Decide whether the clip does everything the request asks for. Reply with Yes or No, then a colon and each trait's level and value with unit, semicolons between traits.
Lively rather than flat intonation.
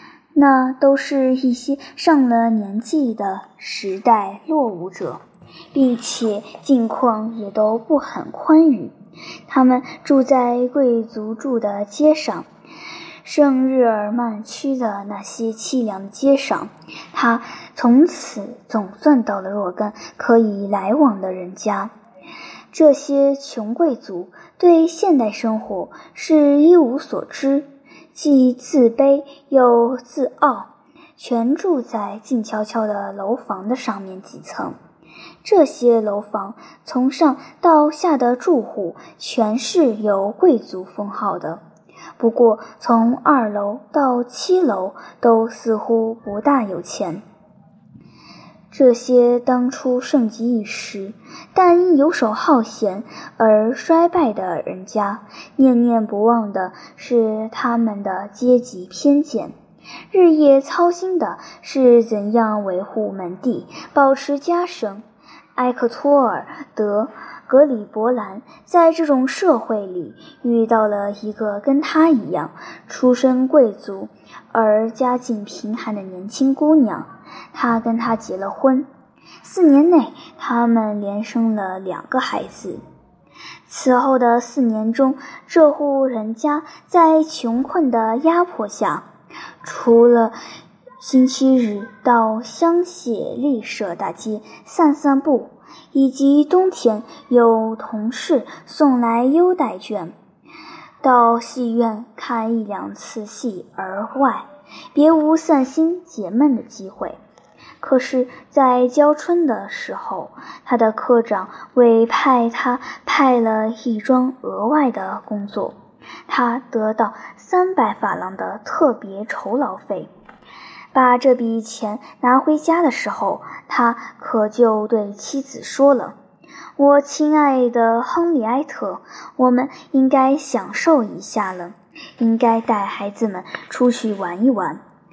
No: average, 4.6 semitones